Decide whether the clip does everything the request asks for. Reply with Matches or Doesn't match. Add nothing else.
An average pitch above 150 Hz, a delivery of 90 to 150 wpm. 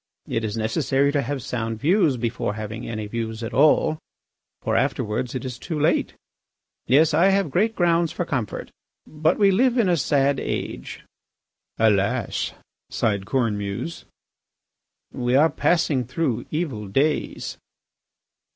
Doesn't match